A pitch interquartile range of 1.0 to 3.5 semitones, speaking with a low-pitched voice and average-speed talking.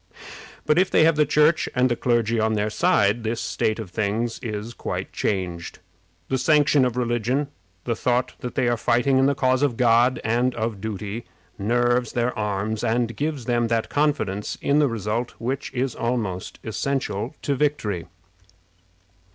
Yes: average, 3.2 semitones; low, 120 Hz; average, 165 wpm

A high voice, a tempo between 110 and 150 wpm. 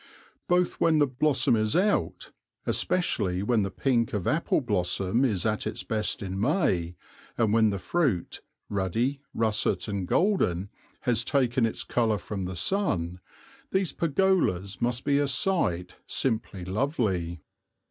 No: low, 115 Hz; average, 140 wpm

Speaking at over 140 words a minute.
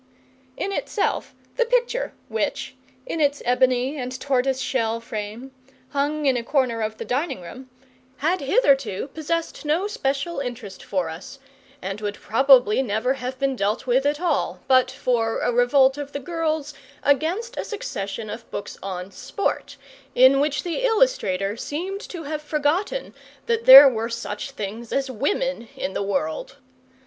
Yes: average, 155 wpm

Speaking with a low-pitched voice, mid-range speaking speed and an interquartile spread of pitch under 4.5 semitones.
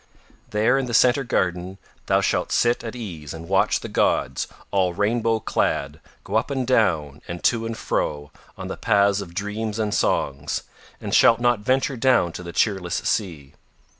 No: low, 105 Hz; average, 175 wpm; average, 4.9 semitones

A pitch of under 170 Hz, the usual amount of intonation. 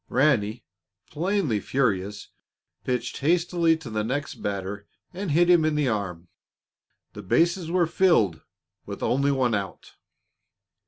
No: low, 135 Hz; wide, 8.3 semitones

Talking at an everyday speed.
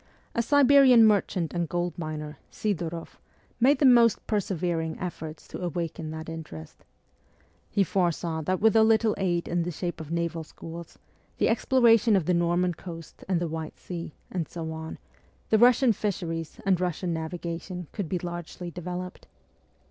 Yes: average, 155 wpm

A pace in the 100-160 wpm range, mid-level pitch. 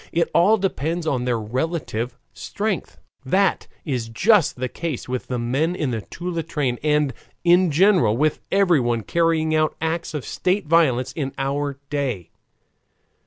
Yes: average, 150 wpm; medium, 150 Hz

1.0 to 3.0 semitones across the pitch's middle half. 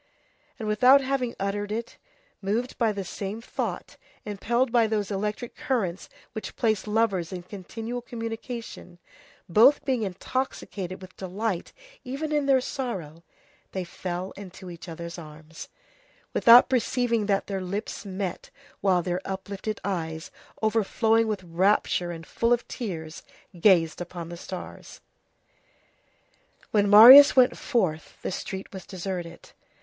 No: average, 4.3 semitones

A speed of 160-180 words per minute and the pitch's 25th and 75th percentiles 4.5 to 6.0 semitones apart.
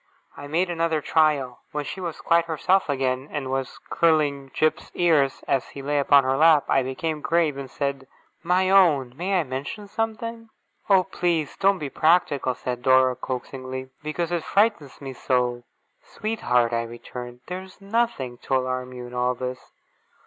Yes: average, 170 wpm; average, 5.0 semitones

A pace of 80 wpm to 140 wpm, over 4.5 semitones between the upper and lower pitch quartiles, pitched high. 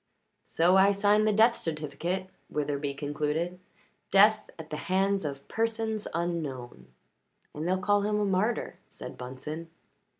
No: slow, 135 wpm; wide, 5.4 semitones; medium, 175 Hz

